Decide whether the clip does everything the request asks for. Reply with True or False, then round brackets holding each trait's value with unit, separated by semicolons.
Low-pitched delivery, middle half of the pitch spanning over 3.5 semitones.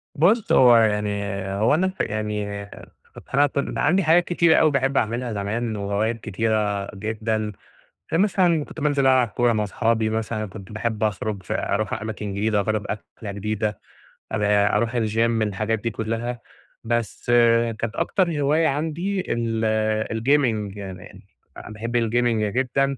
True (110 Hz; 4.1 semitones)